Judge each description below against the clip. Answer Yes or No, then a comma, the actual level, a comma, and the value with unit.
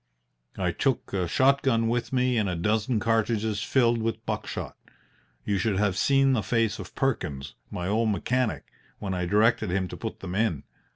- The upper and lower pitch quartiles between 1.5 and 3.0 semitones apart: No, average, 3.6 semitones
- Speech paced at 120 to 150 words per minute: No, average, 185 wpm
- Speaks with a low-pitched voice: Yes, low, 110 Hz